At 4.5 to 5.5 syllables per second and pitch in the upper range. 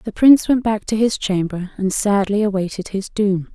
Yes: 4.9 syllables/s; high, 205 Hz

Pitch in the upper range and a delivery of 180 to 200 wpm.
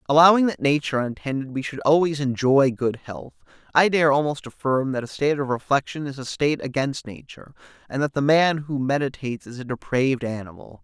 No: low, 135 Hz; average, 190 wpm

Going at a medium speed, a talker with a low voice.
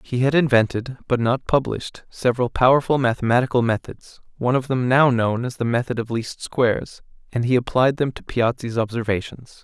Yes: average, 175 wpm; low, 125 Hz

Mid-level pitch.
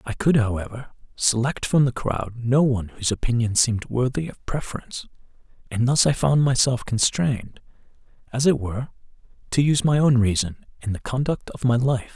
No: low, 125 Hz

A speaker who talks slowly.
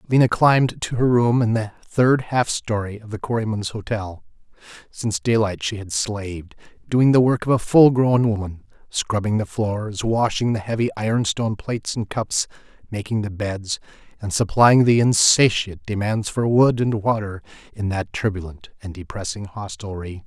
No: average, 165 wpm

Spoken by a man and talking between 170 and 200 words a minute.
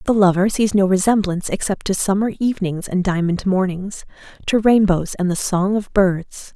No: female; average, 175 wpm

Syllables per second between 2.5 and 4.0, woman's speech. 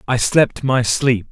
No: 3.6 syllables/s; male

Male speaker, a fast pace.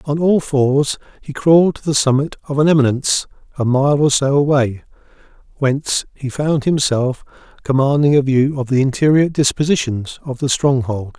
No: male; average, 160 wpm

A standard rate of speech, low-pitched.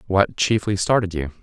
Yes: average, 170 wpm; very low, 95 Hz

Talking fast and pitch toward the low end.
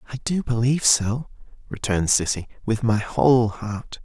No: average, 150 wpm; low, 115 Hz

